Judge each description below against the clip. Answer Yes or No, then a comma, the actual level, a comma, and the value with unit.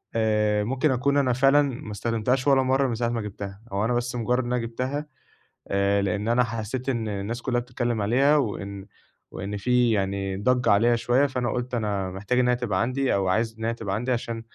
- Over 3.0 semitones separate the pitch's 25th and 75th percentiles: Yes, average, 3.4 semitones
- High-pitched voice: No, low, 120 Hz